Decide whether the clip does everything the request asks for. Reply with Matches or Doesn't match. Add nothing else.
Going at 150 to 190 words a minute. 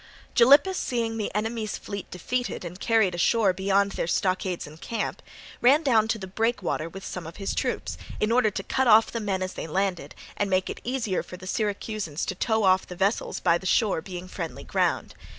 Doesn't match